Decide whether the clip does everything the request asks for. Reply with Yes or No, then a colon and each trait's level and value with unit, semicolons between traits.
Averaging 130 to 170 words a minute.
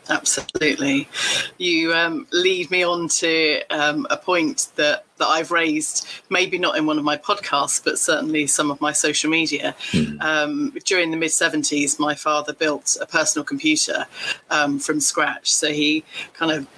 Yes: average, 165 wpm